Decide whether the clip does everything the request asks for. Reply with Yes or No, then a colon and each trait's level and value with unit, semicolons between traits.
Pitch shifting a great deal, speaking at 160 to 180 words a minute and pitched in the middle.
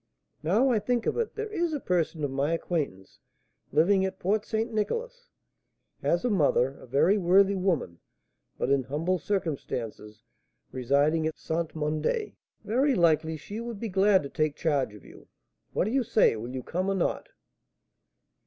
Yes: wide, 6.8 semitones; average, 170 wpm; medium, 175 Hz